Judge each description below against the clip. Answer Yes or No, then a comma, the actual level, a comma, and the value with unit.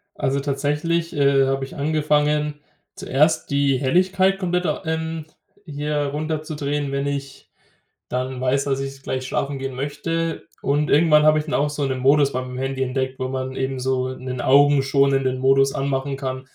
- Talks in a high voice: No, medium, 140 Hz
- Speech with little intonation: Yes, narrow, 2.1 semitones